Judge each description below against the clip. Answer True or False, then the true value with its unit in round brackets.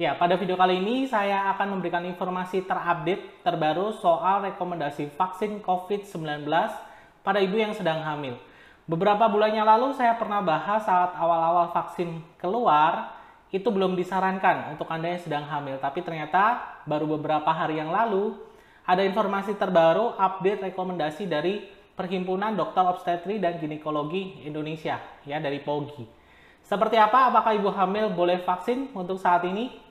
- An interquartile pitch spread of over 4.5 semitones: False (3.7 semitones)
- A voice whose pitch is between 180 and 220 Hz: True (185 Hz)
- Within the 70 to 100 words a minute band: False (140 wpm)